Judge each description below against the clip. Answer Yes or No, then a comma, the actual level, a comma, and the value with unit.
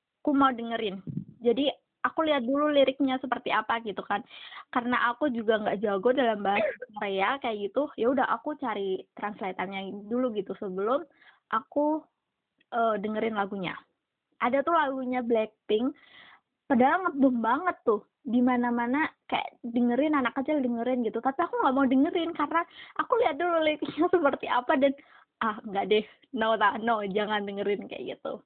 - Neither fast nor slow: No, fast, 155 wpm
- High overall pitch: Yes, very high, 250 Hz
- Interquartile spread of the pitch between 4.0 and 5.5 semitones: Yes, average, 5.2 semitones